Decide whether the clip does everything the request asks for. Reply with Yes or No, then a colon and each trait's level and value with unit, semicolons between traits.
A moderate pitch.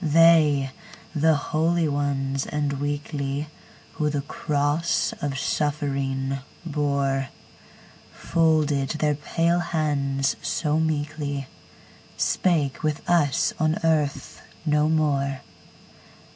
Yes: medium, 145 Hz